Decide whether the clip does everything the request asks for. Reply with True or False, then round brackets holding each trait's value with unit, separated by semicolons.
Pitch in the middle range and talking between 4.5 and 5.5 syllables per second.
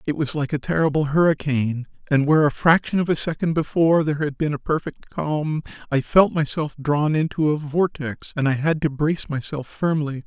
True (150 Hz; 5.4 syllables/s)